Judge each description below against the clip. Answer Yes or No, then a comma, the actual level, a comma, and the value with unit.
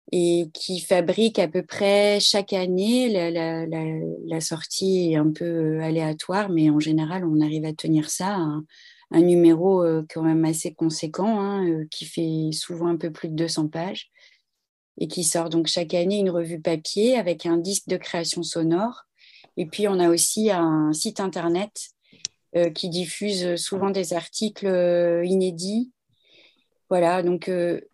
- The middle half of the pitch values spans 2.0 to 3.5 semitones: Yes, average, 2.8 semitones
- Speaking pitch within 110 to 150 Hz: No, medium, 175 Hz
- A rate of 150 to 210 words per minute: Yes, average, 160 wpm